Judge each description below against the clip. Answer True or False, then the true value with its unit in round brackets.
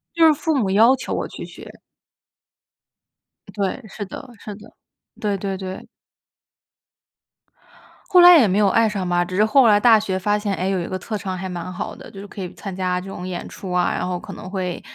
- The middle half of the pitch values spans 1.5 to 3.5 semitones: True (2.7 semitones)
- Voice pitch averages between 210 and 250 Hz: False (195 Hz)